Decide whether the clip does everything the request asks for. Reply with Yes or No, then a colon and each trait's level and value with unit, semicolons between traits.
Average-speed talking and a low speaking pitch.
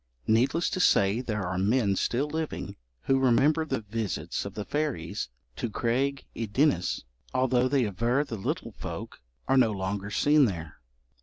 Yes: average, 160 wpm; low, 120 Hz